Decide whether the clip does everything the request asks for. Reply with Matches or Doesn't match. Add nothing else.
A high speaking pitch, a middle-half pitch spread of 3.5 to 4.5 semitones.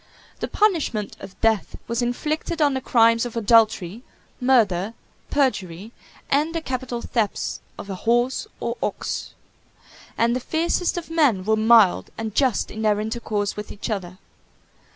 Matches